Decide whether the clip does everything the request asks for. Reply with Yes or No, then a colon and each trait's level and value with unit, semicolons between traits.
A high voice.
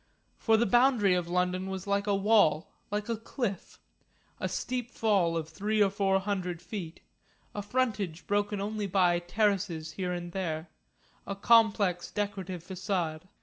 Yes: high, 195 Hz